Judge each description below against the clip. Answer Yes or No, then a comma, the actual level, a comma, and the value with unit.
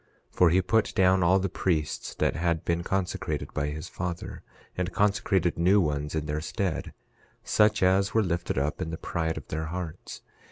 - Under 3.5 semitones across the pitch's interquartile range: Yes, average, 3.0 semitones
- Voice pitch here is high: No, very low, 85 Hz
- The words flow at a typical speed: Yes, average, 190 wpm